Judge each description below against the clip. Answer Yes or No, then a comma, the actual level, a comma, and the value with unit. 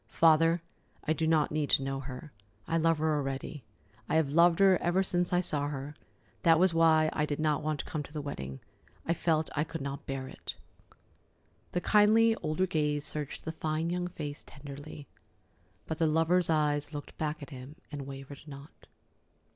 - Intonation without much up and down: Yes, narrow, 2.3 semitones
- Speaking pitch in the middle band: Yes, medium, 155 Hz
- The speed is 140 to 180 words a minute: No, average, 190 wpm